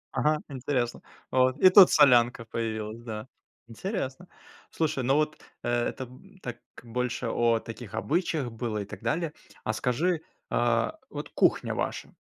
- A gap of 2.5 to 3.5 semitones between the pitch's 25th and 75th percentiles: No, average, 4.6 semitones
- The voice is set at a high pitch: No, low, 125 Hz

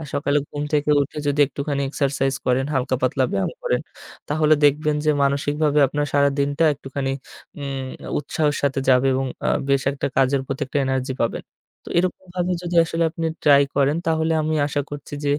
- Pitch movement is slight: Yes, narrow, 1.9 semitones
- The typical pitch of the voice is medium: Yes, medium, 145 Hz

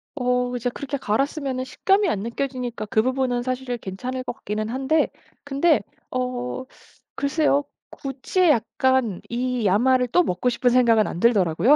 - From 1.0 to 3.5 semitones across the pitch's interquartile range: Yes, narrow, 2.4 semitones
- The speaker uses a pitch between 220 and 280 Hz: Yes, very high, 250 Hz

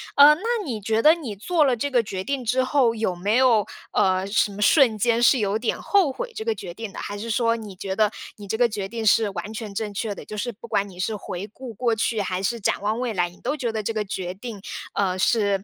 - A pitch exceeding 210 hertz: Yes, high, 220 Hz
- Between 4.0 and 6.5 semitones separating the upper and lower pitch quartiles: No, average, 3.4 semitones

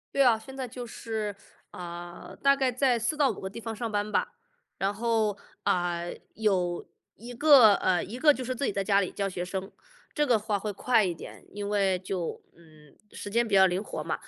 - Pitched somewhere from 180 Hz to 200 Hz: No, high, 210 Hz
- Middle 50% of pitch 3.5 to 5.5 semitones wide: Yes, average, 4.0 semitones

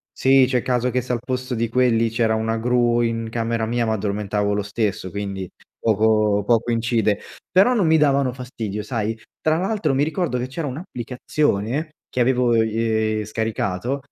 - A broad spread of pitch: No, average, 2.7 semitones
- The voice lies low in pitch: Yes, low, 115 Hz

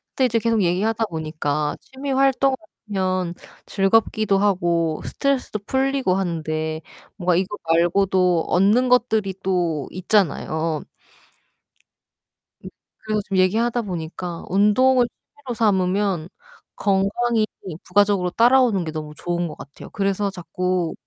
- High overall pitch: Yes, high, 195 Hz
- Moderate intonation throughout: Yes, average, 4.4 semitones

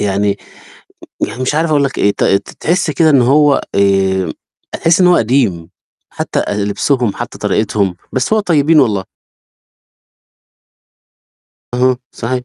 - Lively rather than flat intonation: Yes, wide, 6.7 semitones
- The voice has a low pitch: Yes, low, 125 Hz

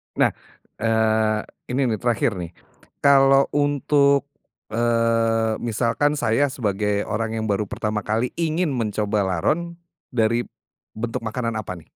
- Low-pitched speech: Yes, low, 115 Hz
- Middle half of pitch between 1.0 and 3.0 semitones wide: No, average, 4.0 semitones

